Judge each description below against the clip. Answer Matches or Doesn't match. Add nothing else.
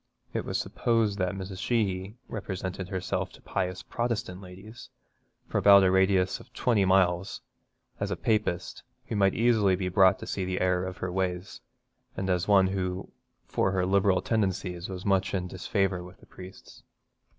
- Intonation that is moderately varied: Doesn't match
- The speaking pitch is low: Matches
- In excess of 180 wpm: Doesn't match